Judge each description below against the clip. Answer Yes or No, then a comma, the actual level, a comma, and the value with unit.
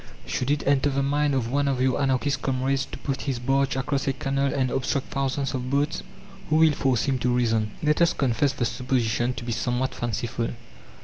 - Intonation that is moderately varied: No, narrow, 2.0 semitones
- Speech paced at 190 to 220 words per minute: Yes, fast, 205 wpm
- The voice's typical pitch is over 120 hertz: Yes, low, 135 Hz